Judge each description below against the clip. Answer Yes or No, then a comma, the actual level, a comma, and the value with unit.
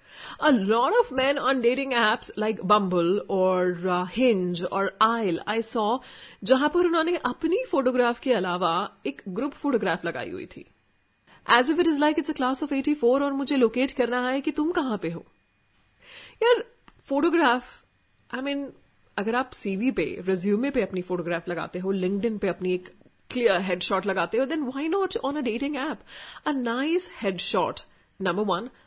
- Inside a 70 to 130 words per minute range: No, average, 170 wpm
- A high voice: Yes, high, 240 Hz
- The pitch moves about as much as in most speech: No, wide, 6.5 semitones